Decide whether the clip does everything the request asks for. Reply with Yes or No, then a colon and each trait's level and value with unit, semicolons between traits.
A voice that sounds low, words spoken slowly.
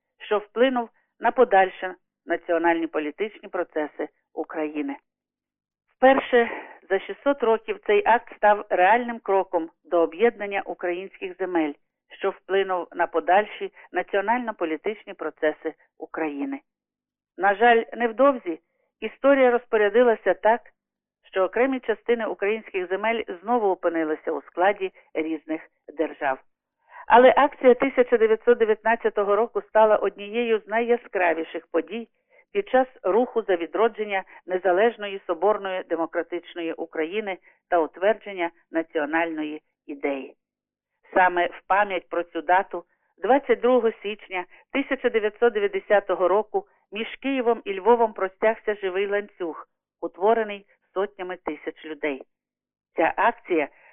No: high, 200 Hz; slow, 100 wpm